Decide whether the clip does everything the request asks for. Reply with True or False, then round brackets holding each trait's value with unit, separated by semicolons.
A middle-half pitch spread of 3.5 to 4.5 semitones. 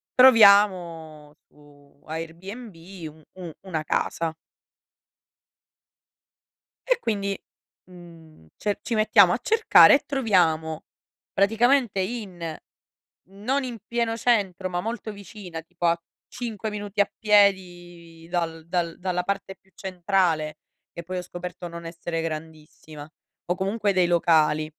True (3.9 semitones)